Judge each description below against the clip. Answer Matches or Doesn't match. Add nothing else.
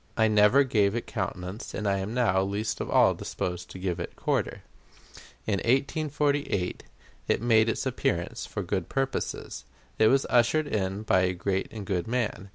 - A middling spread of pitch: Matches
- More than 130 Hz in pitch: Doesn't match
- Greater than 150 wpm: Matches